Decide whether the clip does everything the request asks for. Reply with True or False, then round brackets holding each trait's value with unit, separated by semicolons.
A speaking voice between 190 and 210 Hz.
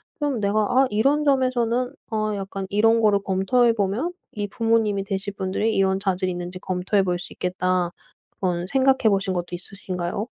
True (200 Hz)